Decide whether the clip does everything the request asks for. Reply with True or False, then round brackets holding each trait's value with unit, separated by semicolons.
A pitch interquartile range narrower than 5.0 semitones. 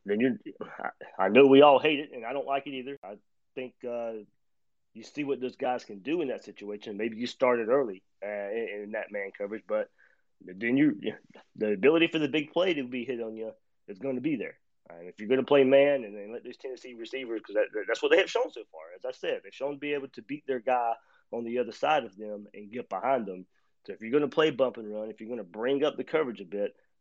False (5.6 semitones)